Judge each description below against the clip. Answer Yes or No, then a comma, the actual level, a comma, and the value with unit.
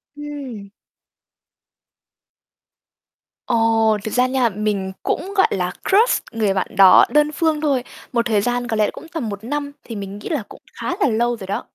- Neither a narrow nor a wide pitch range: No, wide, 5.7 semitones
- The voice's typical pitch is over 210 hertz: Yes, high, 235 Hz